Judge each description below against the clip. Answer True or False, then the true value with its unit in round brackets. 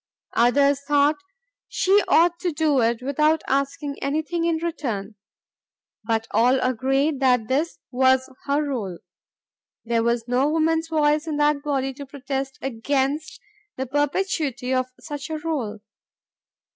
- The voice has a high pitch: True (280 Hz)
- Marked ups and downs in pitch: False (3.1 semitones)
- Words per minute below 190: True (135 wpm)